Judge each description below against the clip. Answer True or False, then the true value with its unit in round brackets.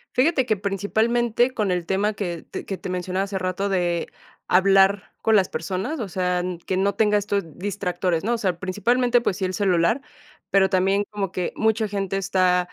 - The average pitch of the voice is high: True (195 Hz)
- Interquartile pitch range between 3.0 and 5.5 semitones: False (2.4 semitones)